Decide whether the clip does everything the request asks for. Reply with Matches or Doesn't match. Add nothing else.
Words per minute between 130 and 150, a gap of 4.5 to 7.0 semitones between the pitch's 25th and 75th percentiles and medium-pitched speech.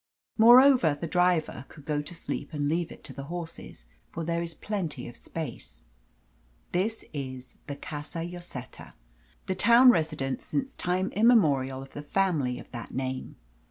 Doesn't match